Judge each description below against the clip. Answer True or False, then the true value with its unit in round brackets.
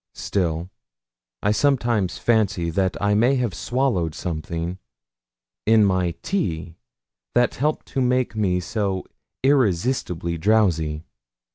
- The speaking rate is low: True (110 wpm)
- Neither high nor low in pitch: False (100 Hz)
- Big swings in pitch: True (5.9 semitones)